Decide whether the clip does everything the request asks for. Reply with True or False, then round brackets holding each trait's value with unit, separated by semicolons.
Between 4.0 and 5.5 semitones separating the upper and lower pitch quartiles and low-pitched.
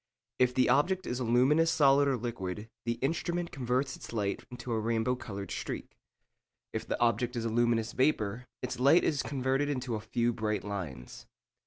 False (3.3 semitones; 125 Hz)